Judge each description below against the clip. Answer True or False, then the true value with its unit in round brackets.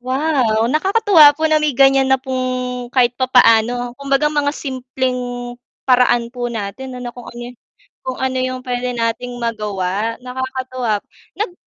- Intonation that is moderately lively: False (1.7 semitones)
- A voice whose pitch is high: True (255 Hz)